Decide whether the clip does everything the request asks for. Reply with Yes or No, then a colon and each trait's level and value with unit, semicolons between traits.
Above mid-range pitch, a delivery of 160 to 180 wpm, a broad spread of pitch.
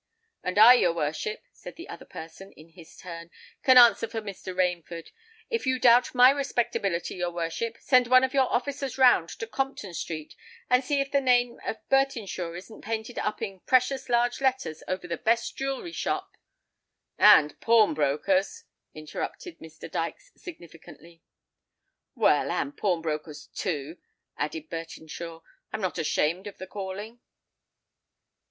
No: high, 210 Hz; average, 145 wpm; wide, 7.3 semitones